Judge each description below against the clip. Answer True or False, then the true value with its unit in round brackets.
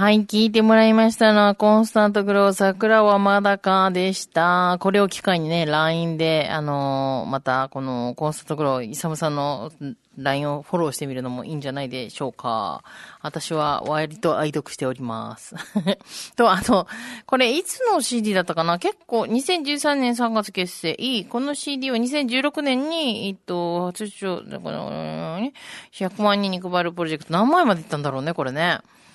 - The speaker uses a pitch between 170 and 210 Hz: True (185 Hz)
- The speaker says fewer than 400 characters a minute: True (335 characters per minute)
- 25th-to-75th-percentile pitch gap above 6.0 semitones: True (6.5 semitones)